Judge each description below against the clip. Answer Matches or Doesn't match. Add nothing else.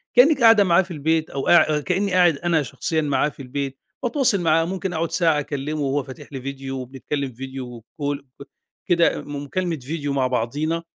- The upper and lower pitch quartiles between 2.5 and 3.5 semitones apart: Doesn't match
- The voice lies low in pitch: Doesn't match